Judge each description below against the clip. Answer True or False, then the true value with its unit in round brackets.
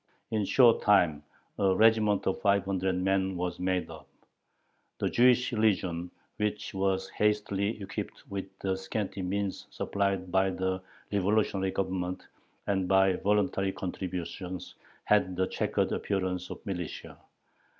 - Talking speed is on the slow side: True (130 wpm)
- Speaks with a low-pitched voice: True (95 Hz)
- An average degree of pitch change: False (1.6 semitones)